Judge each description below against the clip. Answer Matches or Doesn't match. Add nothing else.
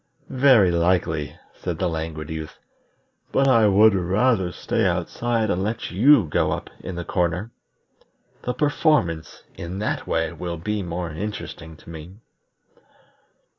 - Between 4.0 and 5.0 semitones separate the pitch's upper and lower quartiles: Matches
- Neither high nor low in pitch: Doesn't match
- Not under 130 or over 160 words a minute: Matches